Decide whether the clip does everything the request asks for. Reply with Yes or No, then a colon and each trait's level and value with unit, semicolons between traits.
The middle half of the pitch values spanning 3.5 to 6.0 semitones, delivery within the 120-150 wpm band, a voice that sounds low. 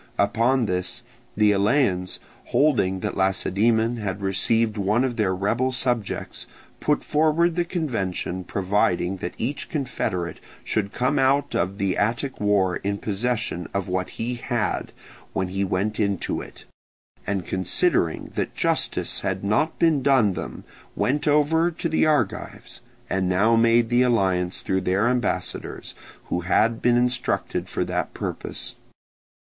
Yes: average, 4.9 semitones; average, 140 wpm; low, 110 Hz